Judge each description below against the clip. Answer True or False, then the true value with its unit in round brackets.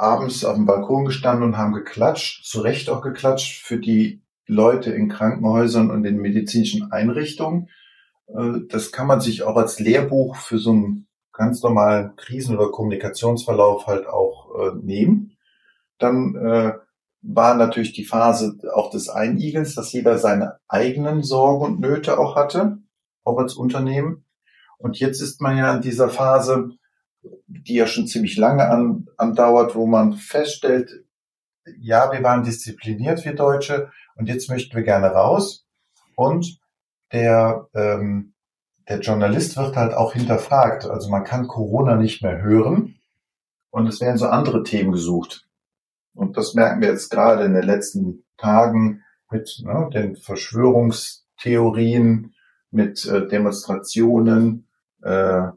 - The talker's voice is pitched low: True (115 Hz)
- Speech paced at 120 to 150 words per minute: True (140 wpm)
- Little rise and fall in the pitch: False (3.6 semitones)